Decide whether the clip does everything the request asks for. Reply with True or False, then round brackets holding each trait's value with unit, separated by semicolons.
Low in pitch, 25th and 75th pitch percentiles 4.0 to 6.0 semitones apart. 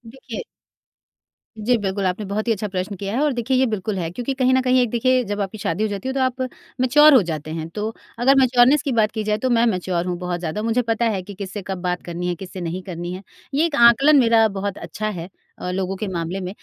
False (210 Hz; 5.0 semitones)